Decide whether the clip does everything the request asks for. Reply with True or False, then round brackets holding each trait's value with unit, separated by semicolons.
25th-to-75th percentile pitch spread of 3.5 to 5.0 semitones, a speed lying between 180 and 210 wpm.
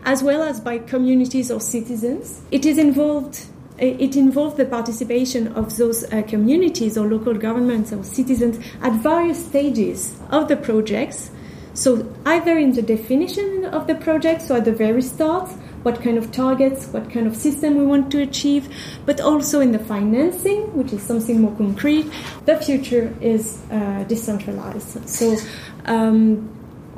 False (4.2 semitones; 160 wpm)